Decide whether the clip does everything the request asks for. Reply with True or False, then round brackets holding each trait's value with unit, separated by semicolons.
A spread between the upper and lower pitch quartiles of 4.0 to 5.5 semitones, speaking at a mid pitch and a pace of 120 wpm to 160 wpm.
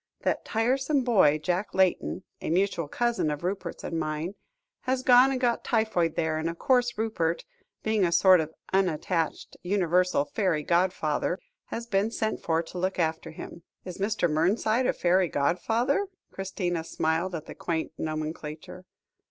True (5.2 semitones; 180 Hz; 155 wpm)